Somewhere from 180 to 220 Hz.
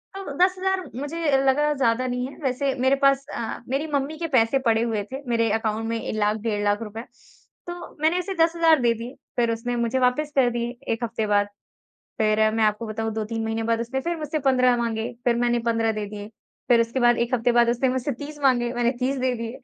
No: high, 240 Hz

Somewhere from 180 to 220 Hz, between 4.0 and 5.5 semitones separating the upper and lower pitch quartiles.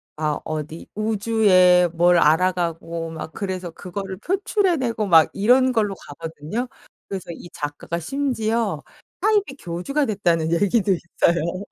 Yes: medium, 185 Hz; average, 5.1 semitones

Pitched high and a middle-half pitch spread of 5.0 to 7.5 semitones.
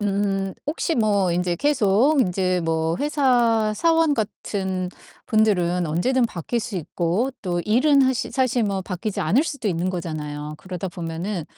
Yes: high, 195 Hz; wide, 5.5 semitones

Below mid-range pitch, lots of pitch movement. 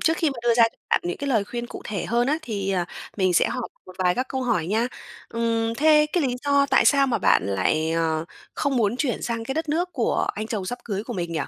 No: high, 230 Hz; wide, 6.0 semitones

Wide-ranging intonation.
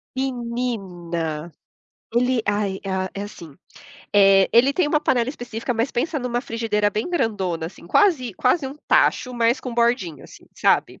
No: average, 4.5 semitones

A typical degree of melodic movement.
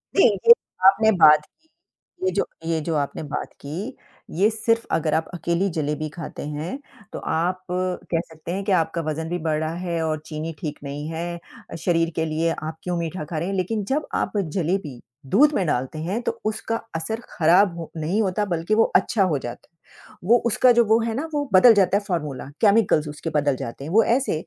Yes: average, 4.7 semitones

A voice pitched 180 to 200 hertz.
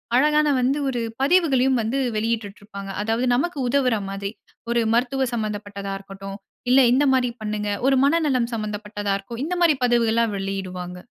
No: high, 230 Hz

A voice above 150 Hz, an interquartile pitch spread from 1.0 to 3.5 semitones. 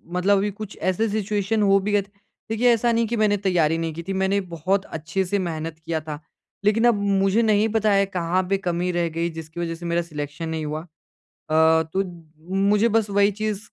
No: high, 190 Hz; average, 3.9 semitones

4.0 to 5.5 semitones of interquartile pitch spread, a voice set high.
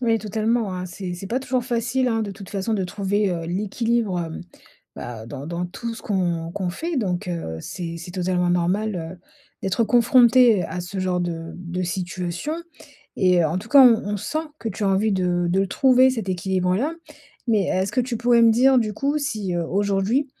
Yes: average, 4.5 semitones; high, 195 Hz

